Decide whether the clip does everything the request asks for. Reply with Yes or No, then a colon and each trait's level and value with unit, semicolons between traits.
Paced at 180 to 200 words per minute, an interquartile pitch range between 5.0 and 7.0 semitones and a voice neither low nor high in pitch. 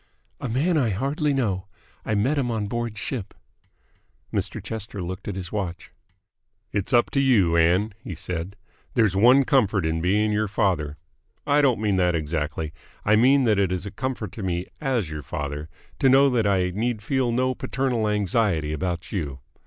No: average, 185 wpm; wide, 5.4 semitones; low, 105 Hz